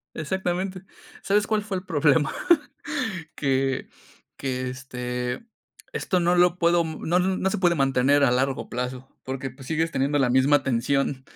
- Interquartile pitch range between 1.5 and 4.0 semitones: No, average, 5.1 semitones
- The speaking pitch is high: No, medium, 140 Hz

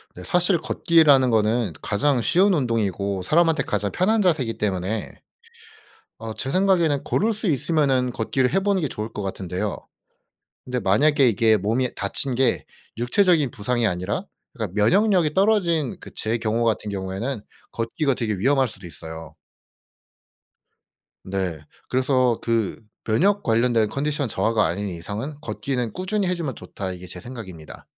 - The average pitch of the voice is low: Yes, low, 120 Hz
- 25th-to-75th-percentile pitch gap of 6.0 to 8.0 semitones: Yes, wide, 6.8 semitones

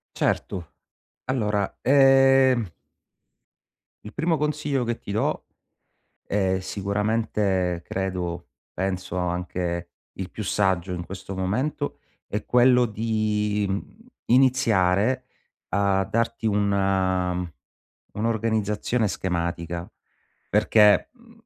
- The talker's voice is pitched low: Yes, low, 105 Hz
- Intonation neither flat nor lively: Yes, average, 3.9 semitones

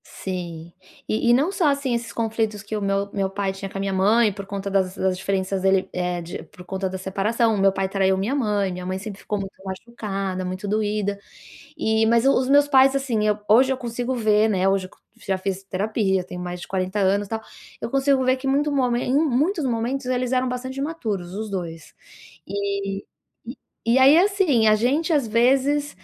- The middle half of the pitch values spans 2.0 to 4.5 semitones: No, average, 4.9 semitones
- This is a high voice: Yes, high, 210 Hz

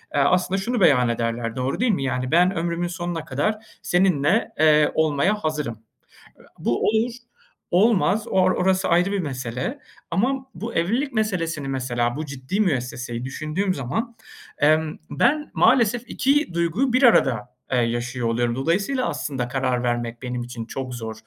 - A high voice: No, medium, 155 Hz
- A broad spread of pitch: Yes, wide, 7.9 semitones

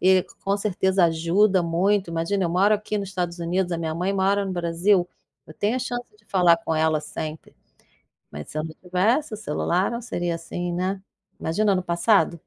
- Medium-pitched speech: Yes, medium, 180 Hz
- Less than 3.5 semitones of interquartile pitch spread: Yes, average, 3.0 semitones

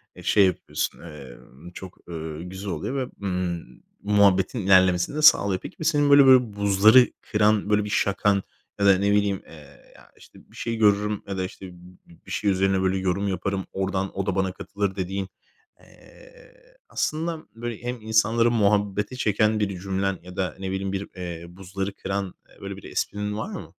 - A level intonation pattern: Yes, narrow, 2.1 semitones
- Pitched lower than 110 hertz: Yes, low, 100 Hz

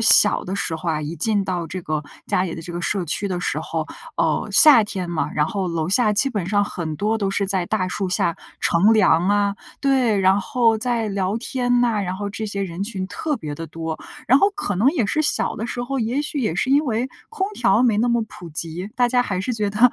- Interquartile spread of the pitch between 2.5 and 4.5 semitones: No, average, 4.9 semitones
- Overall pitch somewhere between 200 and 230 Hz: Yes, high, 205 Hz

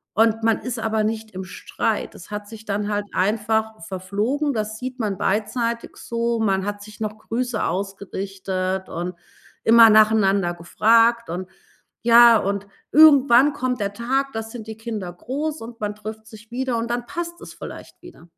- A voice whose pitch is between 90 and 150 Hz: No, high, 220 Hz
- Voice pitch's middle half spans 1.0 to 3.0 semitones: Yes, average, 2.7 semitones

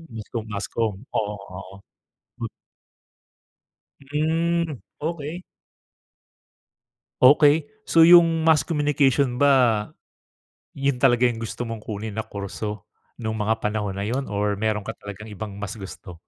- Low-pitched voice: Yes, low, 115 Hz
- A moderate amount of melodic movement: No, wide, 5.8 semitones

